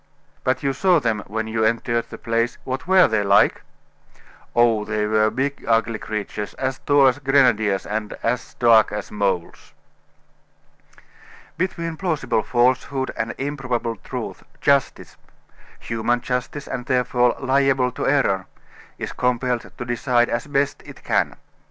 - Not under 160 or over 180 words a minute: No, average, 140 wpm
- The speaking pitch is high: No, low, 120 Hz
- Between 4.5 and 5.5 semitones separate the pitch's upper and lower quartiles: No, average, 3.4 semitones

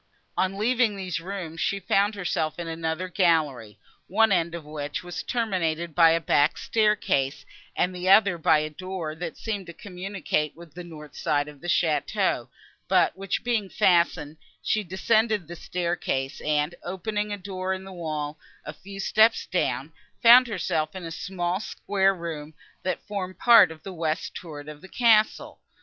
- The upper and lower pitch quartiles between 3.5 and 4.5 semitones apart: Yes, average, 3.8 semitones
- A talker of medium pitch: Yes, medium, 175 Hz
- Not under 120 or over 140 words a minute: No, average, 170 wpm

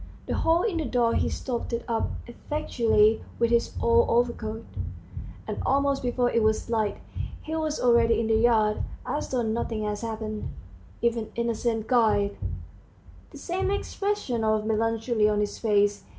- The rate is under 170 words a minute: Yes, average, 150 wpm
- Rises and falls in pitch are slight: Yes, narrow, 2.1 semitones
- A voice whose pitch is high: Yes, high, 230 Hz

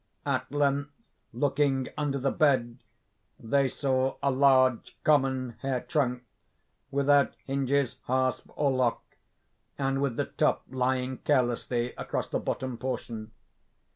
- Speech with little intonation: Yes, narrow, 1.8 semitones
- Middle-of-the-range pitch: No, low, 130 Hz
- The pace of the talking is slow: Yes, slow, 120 wpm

